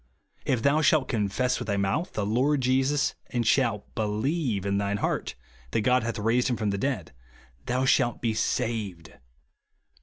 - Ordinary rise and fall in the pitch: Yes, average, 3.9 semitones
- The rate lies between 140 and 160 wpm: No, average, 175 wpm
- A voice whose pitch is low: Yes, low, 115 Hz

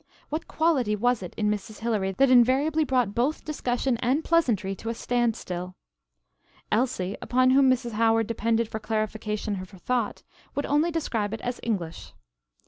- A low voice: No, high, 230 Hz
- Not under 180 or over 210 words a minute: No, average, 160 wpm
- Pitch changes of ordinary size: Yes, average, 3.4 semitones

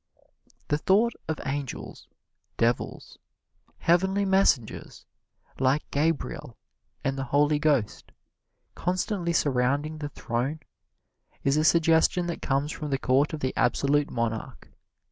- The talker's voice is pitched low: No, medium, 145 Hz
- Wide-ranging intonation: No, average, 3.5 semitones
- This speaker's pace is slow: Yes, slow, 115 wpm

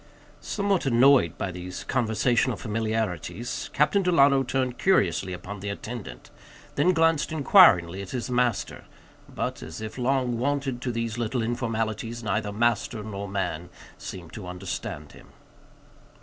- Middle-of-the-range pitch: No, low, 115 Hz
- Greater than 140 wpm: No, slow, 135 wpm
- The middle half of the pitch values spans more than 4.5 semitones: Yes, average, 4.9 semitones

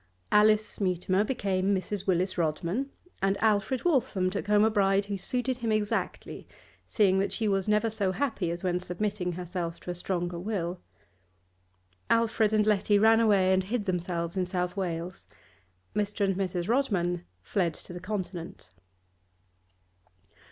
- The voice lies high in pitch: Yes, high, 195 Hz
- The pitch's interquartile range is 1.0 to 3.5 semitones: Yes, average, 2.9 semitones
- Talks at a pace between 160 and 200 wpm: No, average, 150 wpm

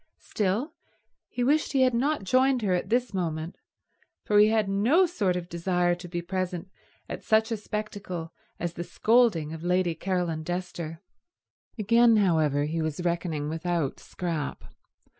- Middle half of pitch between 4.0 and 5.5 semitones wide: Yes, average, 4.6 semitones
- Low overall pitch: No, medium, 180 Hz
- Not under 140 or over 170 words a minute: Yes, average, 155 wpm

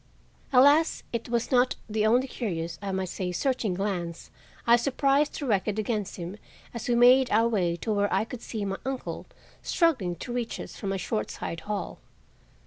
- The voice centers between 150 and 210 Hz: No, high, 220 Hz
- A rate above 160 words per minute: Yes, average, 180 wpm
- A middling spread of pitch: Yes, average, 4.6 semitones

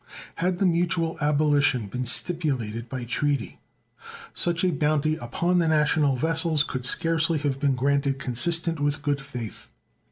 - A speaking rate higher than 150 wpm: No, average, 140 wpm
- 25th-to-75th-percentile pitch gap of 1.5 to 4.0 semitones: Yes, average, 3.5 semitones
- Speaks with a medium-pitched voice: Yes, medium, 145 Hz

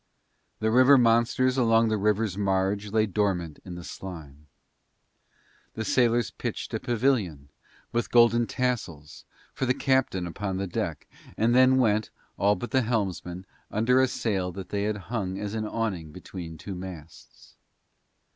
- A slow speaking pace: No, average, 150 wpm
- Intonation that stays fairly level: No, average, 4.1 semitones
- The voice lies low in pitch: Yes, low, 105 Hz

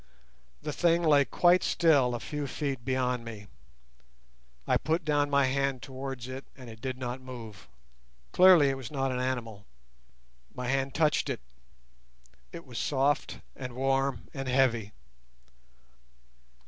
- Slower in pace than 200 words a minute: Yes, average, 140 wpm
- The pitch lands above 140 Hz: No, low, 135 Hz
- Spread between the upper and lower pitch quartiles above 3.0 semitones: No, narrow, 2.4 semitones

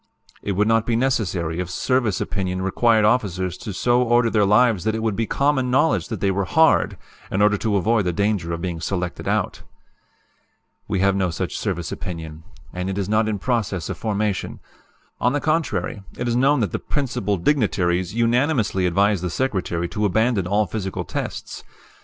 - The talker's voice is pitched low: Yes, low, 105 Hz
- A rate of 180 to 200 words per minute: Yes, average, 185 wpm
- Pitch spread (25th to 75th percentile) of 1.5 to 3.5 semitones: No, average, 4.3 semitones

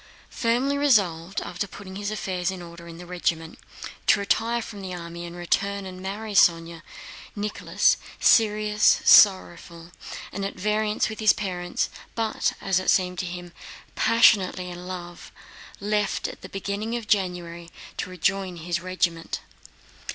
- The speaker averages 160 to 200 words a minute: No, average, 145 wpm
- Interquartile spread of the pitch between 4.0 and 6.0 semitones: No, average, 3.1 semitones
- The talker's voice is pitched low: No, medium, 185 Hz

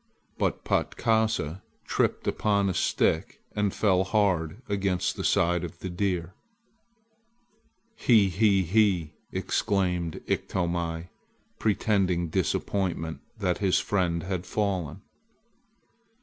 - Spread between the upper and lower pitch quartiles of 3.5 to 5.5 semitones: No, average, 2.8 semitones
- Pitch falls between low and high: No, very low, 95 Hz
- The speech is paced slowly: Yes, slow, 100 wpm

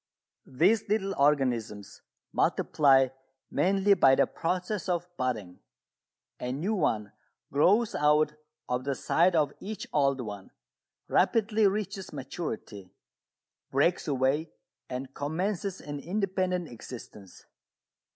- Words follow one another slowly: Yes, slow, 105 wpm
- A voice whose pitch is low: No, medium, 150 Hz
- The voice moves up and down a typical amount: No, wide, 6.5 semitones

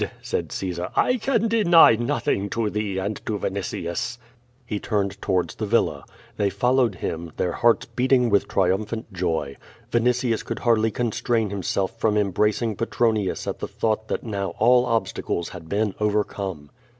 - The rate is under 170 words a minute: Yes, average, 150 wpm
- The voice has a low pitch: Yes, low, 105 Hz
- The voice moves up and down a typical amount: Yes, average, 3.3 semitones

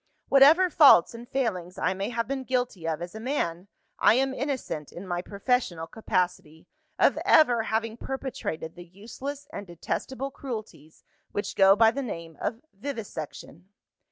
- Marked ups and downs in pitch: Yes, wide, 7.0 semitones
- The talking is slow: No, average, 155 wpm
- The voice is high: Yes, high, 220 Hz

